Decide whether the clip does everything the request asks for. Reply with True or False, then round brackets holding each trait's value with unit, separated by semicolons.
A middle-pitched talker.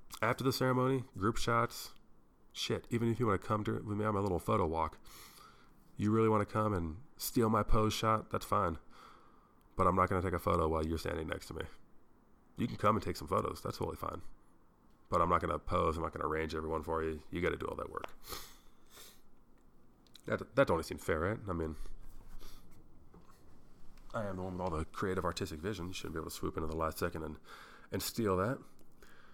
False (95 Hz)